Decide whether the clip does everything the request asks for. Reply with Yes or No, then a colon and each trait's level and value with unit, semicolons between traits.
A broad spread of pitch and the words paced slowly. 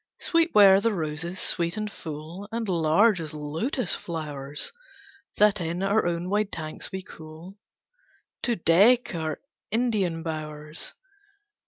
No: average, 4.9 semitones; slow, 130 wpm